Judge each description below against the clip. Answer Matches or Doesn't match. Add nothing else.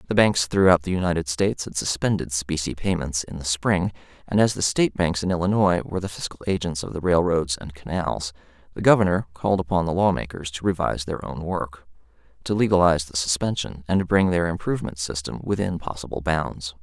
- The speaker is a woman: Doesn't match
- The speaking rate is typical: Matches